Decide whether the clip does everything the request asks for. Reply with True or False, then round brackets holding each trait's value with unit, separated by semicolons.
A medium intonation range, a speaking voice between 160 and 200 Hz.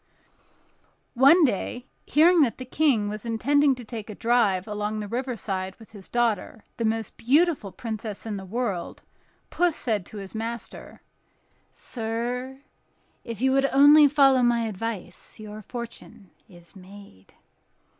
False (3.9 semitones; 230 Hz)